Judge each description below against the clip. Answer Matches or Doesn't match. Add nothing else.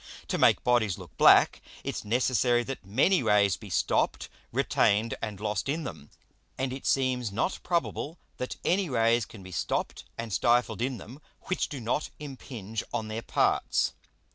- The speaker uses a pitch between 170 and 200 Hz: Doesn't match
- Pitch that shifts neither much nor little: Matches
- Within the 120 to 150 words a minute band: Doesn't match